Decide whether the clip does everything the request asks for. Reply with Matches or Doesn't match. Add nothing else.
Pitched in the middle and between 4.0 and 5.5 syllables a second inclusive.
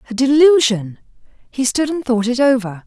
Doesn't match